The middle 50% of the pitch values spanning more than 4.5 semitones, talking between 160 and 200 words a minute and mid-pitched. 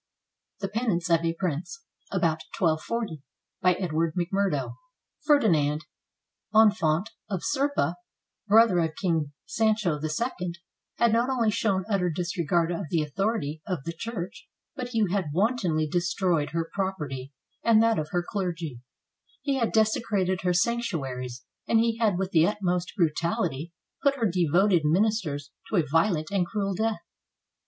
No: average, 5.1 semitones; average, 140 wpm; medium, 180 Hz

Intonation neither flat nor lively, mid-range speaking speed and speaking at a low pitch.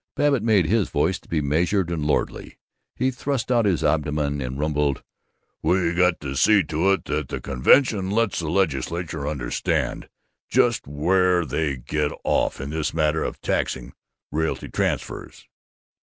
Yes: average, 4.6 semitones; average, 155 wpm; very low, 80 Hz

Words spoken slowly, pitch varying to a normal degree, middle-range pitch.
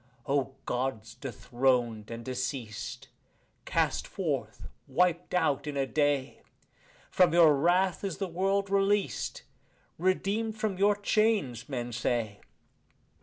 No: slow, 115 wpm; wide, 7.6 semitones; medium, 150 Hz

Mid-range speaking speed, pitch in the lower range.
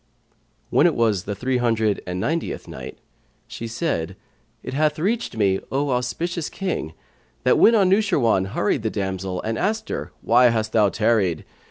Yes: average, 160 wpm; low, 115 Hz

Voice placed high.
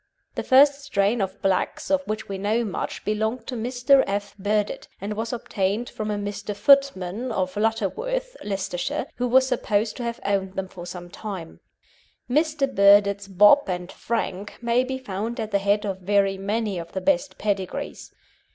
Yes: high, 210 Hz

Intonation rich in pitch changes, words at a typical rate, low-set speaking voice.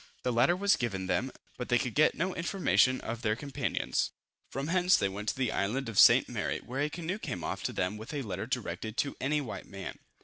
No: wide, 5.8 semitones; fast, 230 wpm; low, 125 Hz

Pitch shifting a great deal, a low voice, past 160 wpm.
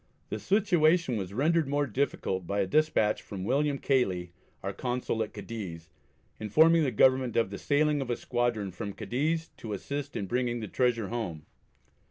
Yes: wide, 5.9 semitones; low, 120 Hz; average, 170 wpm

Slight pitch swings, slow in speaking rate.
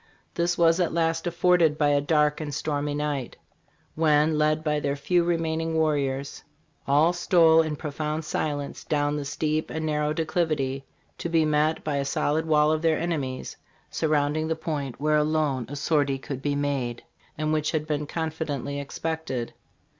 No: narrow, 1.8 semitones; average, 165 wpm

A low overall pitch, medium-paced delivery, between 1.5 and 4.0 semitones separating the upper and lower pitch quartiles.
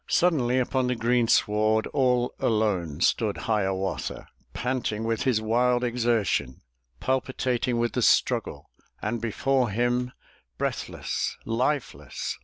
No: low, 120 Hz; slow, 105 wpm; narrow, 2.6 semitones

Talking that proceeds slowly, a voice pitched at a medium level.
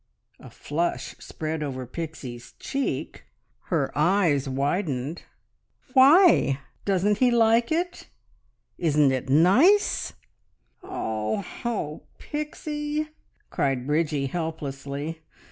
Yes: slow, 90 wpm; medium, 160 Hz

